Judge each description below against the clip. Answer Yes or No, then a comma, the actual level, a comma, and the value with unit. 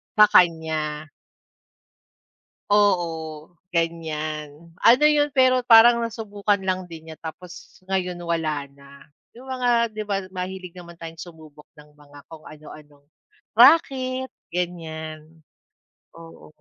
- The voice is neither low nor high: Yes, medium, 170 Hz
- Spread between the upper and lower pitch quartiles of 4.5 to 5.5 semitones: Yes, average, 4.8 semitones